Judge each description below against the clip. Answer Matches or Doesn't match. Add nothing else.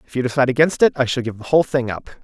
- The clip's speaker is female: Doesn't match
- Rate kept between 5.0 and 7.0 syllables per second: Doesn't match